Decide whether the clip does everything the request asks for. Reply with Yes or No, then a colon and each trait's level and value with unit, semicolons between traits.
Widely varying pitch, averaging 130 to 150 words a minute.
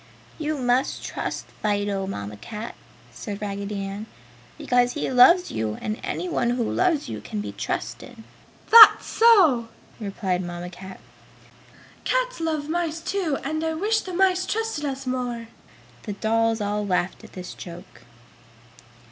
Yes: wide, 8.2 semitones; average, 140 wpm